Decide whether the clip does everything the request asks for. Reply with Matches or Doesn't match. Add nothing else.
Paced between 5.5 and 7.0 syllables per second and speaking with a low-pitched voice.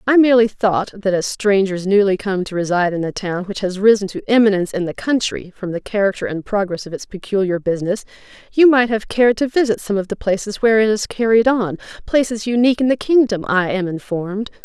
Doesn't match